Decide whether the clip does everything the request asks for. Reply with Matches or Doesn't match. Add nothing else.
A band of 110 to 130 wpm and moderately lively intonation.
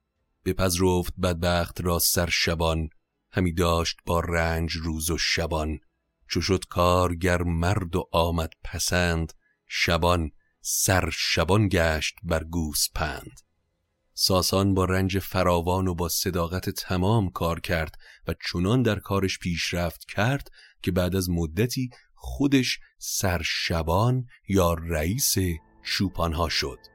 Doesn't match